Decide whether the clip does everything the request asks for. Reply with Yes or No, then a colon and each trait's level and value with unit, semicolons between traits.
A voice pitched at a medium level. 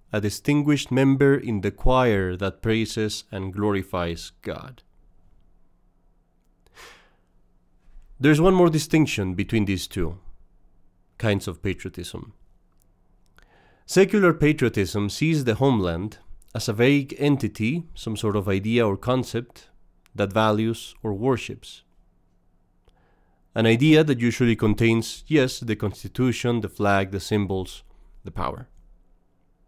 No: low, 105 Hz